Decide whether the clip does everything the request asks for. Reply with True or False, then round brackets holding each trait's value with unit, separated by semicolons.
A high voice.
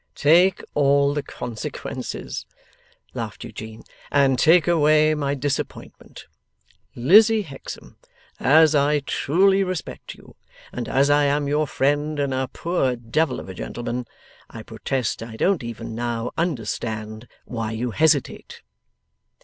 False (140 Hz)